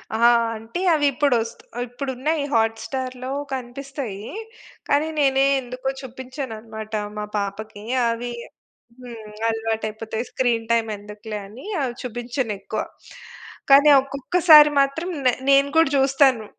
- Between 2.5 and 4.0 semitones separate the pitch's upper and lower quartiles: Yes, average, 3.6 semitones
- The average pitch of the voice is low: No, high, 245 Hz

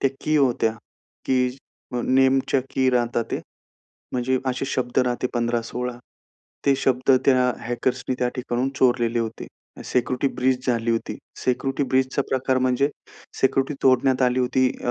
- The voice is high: No, low, 130 Hz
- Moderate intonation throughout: No, narrow, 1.3 semitones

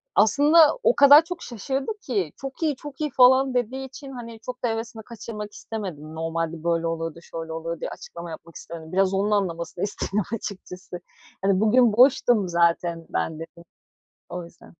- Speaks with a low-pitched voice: No, high, 210 Hz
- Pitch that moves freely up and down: Yes, wide, 7.0 semitones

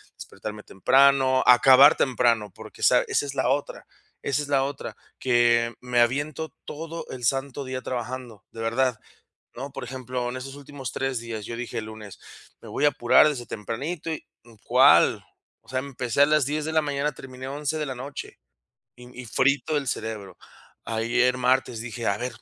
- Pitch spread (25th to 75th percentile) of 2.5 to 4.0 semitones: Yes, average, 2.9 semitones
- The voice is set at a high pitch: No, low, 130 Hz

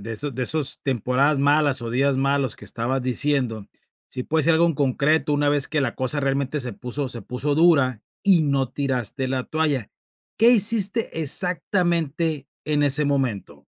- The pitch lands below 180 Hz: Yes, medium, 140 Hz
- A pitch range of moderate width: Yes, average, 3.2 semitones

